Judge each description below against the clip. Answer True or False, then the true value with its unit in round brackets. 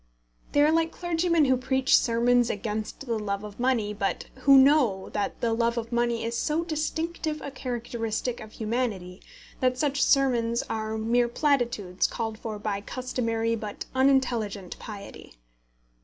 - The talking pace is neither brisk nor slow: True (150 wpm)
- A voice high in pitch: True (235 Hz)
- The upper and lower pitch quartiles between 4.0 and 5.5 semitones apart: False (3.5 semitones)